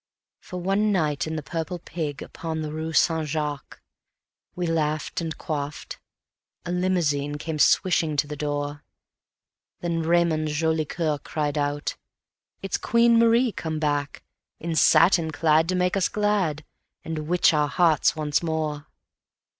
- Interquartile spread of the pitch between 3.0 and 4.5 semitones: No, narrow, 2.6 semitones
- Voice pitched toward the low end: No, medium, 160 Hz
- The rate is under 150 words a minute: Yes, average, 140 wpm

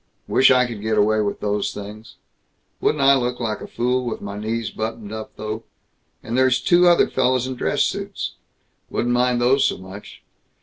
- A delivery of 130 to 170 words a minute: No, average, 185 wpm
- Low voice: Yes, low, 115 Hz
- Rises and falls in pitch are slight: No, average, 3.0 semitones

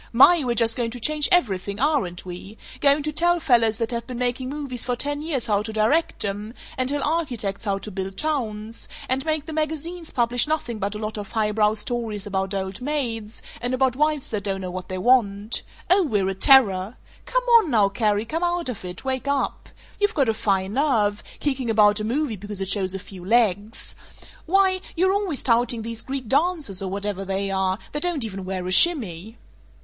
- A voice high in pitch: Yes, high, 230 Hz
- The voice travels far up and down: Yes, wide, 6.1 semitones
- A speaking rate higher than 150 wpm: Yes, fast, 205 wpm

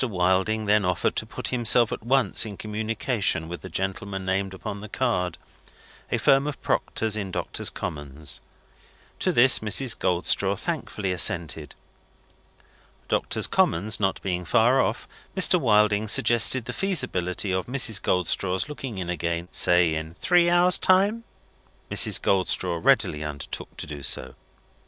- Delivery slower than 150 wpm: Yes, average, 140 wpm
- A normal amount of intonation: Yes, average, 4.9 semitones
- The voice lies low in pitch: Yes, low, 100 Hz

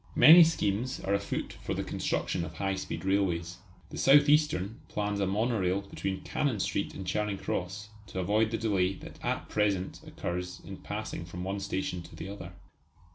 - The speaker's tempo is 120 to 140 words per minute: No, average, 180 wpm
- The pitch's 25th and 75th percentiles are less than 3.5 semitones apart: Yes, narrow, 2.6 semitones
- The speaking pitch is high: No, low, 100 Hz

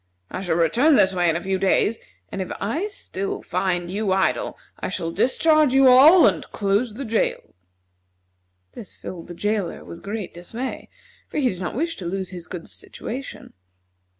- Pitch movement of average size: No, wide, 6.0 semitones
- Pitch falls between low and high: No, high, 200 Hz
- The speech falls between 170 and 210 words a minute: Yes, average, 180 wpm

